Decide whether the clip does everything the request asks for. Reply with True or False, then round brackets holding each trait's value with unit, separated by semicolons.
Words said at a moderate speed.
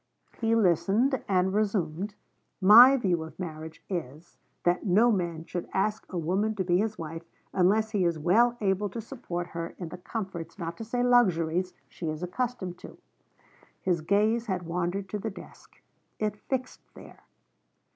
True (165 wpm)